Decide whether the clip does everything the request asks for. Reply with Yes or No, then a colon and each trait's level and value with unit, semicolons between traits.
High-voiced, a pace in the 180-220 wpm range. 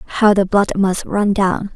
Yes: high, 195 Hz; fast, 205 wpm